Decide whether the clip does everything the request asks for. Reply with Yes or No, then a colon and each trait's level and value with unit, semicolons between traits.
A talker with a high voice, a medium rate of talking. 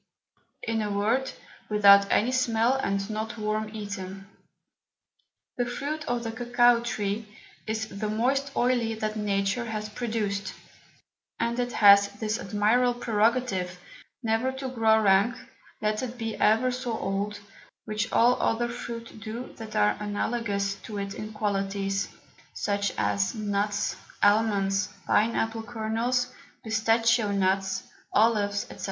No: high, 220 Hz; slow, 130 wpm